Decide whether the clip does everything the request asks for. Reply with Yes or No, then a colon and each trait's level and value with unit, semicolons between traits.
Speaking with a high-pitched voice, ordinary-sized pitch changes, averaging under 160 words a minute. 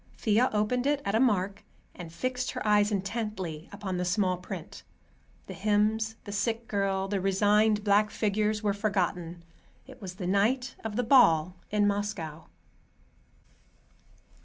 No: high, 205 Hz; narrow, 2.3 semitones; average, 145 wpm